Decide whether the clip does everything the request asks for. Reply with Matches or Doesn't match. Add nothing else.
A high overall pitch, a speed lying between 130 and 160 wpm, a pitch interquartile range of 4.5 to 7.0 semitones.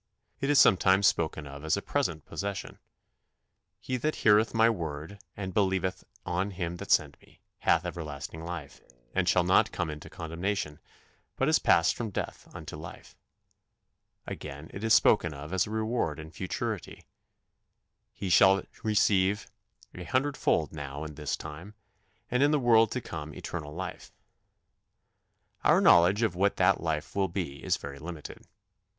Doesn't match